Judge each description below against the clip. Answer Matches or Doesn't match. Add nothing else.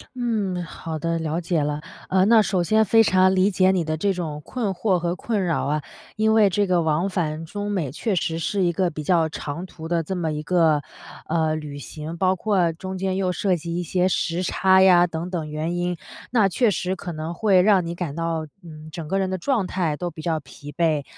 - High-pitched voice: Doesn't match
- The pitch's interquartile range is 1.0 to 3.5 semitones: Matches